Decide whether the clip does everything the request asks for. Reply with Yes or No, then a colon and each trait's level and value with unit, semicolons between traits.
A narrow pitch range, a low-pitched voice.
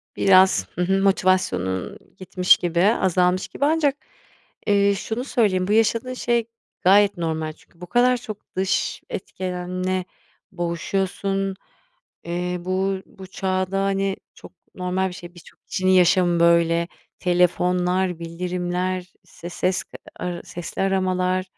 No: narrow, 1.6 semitones; medium, 185 Hz